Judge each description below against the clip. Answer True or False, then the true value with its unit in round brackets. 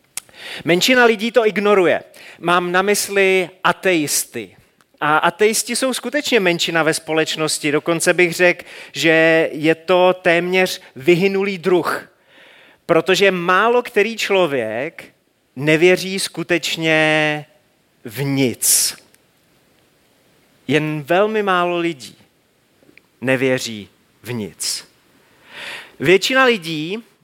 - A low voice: False (175 Hz)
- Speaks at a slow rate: True (90 wpm)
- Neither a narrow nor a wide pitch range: True (4.1 semitones)